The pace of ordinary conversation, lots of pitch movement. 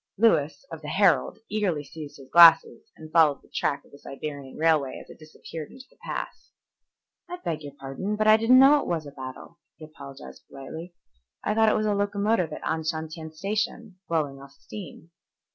Yes: average, 190 wpm; wide, 5.8 semitones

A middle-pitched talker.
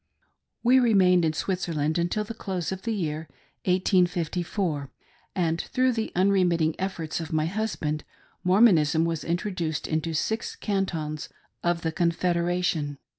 Yes: medium, 175 Hz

